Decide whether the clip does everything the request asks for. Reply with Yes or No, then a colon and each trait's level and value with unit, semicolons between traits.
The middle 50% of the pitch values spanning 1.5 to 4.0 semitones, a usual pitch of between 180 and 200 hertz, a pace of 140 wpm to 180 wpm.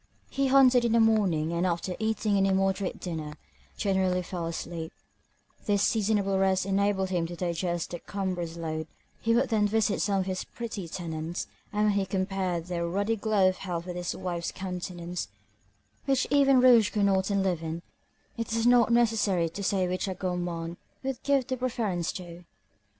Yes: average, 3.7 semitones; high, 190 Hz; average, 170 wpm